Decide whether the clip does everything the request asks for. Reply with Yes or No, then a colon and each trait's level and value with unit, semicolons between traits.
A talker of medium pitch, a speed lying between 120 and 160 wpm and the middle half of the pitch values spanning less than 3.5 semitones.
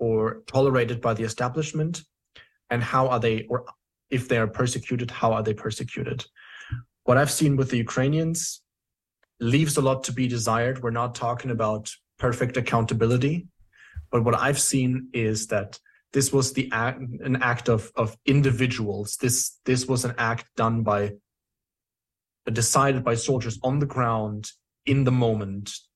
No: low, 125 Hz; average, 155 wpm; narrow, 2.5 semitones